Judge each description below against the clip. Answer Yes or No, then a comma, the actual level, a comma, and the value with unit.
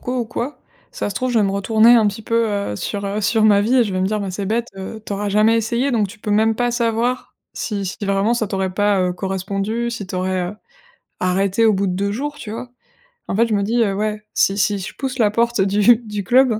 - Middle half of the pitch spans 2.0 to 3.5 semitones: Yes, average, 2.8 semitones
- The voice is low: No, high, 210 Hz